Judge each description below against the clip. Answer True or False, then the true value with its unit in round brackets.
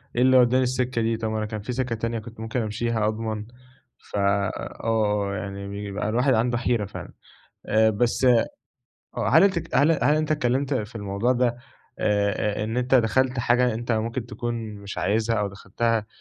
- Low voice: True (115 Hz)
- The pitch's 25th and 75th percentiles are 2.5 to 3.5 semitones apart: True (2.8 semitones)